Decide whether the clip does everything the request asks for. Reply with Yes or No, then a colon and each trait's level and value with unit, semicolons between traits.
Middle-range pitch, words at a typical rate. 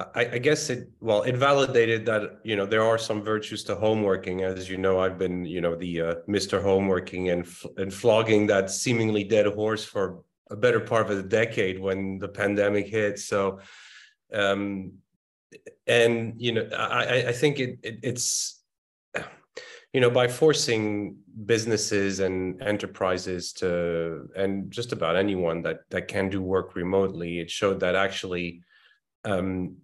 No: low, 100 Hz; average, 160 wpm